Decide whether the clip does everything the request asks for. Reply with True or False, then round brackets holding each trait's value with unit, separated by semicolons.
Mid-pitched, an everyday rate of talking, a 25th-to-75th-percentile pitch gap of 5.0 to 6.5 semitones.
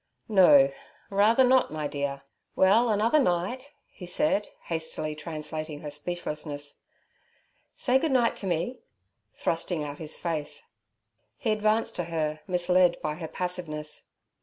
False (175 Hz; 125 wpm; 5.6 semitones)